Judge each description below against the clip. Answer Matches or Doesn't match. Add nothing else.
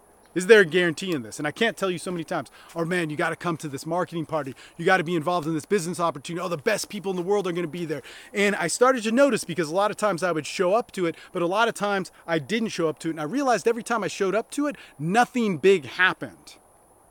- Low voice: Doesn't match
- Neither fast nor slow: Doesn't match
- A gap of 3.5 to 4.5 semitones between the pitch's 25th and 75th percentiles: Matches